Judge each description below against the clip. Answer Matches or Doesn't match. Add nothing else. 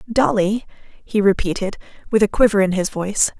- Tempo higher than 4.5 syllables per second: Matches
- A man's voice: Doesn't match